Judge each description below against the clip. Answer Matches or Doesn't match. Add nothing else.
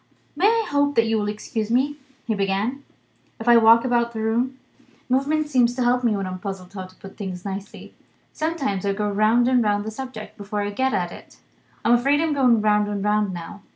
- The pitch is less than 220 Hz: Doesn't match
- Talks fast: Matches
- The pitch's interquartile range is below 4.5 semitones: Matches